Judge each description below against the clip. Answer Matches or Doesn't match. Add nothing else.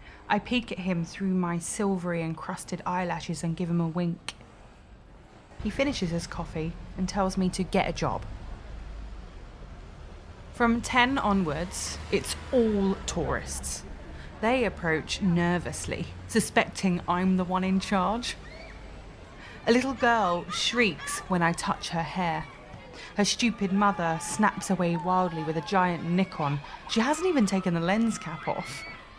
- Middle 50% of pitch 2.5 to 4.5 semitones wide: Matches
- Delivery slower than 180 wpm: Matches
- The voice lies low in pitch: Doesn't match